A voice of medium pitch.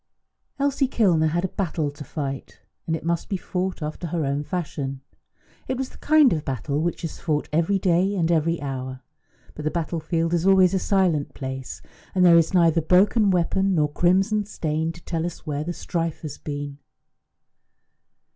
Yes: medium, 165 Hz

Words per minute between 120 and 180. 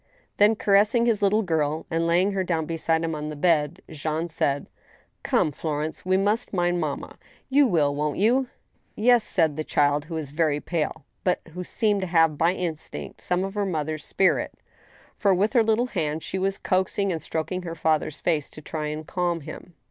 No: average, 200 wpm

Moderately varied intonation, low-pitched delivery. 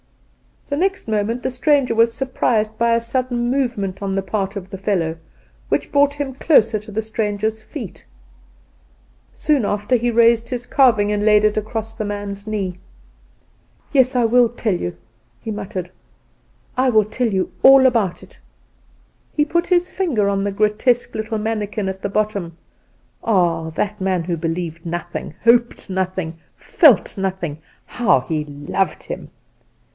No: average, 3.9 semitones; high, 215 Hz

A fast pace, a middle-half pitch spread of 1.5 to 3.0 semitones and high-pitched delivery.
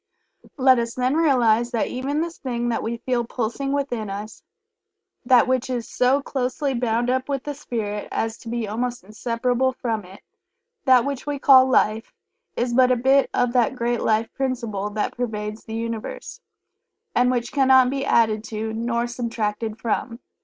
No: average, 170 wpm; narrow, 2.6 semitones; high, 240 Hz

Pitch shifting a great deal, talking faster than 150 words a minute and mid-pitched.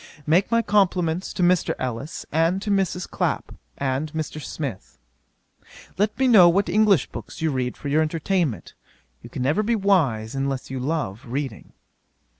Yes: wide, 6.2 semitones; average, 160 wpm; medium, 160 Hz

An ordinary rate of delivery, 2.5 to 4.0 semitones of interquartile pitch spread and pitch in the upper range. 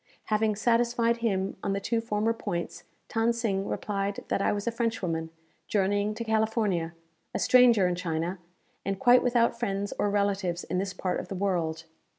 Yes: average, 170 wpm; average, 3.4 semitones; high, 205 Hz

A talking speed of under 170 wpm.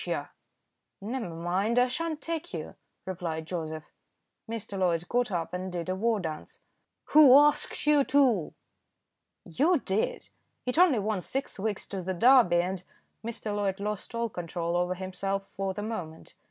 Yes: average, 160 wpm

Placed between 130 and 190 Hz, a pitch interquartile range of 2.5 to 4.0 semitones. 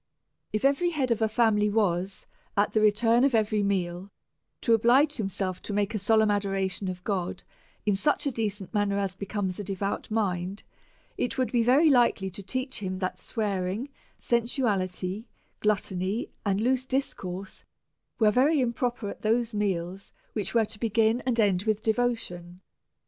No: high, 210 Hz; average, 3.5 semitones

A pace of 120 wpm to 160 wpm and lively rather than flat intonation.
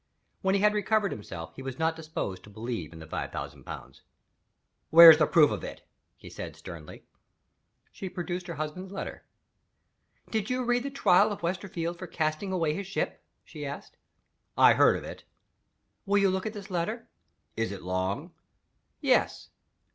No: average, 170 wpm; wide, 6.9 semitones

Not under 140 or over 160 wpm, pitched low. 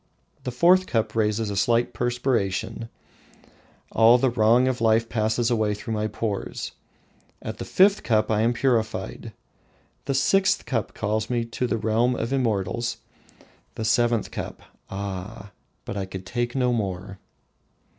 Yes: average, 150 wpm; low, 115 Hz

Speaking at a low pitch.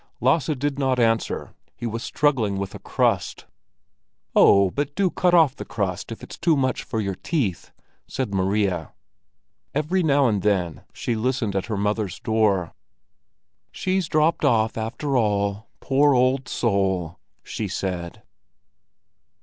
Yes: low, 115 Hz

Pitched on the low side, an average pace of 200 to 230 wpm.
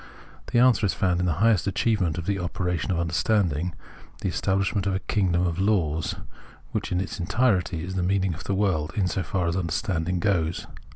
Yes: very low, 90 Hz; fast, 205 wpm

